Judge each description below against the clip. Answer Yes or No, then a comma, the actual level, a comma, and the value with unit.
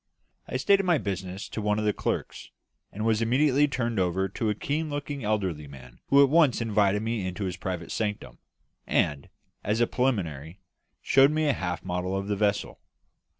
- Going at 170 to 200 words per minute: Yes, average, 185 wpm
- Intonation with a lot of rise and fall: Yes, wide, 5.7 semitones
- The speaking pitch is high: No, low, 105 Hz